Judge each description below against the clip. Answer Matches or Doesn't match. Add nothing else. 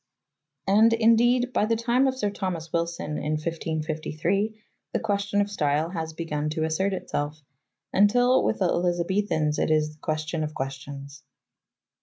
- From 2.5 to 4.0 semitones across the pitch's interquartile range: Doesn't match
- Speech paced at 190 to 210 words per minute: Doesn't match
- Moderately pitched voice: Matches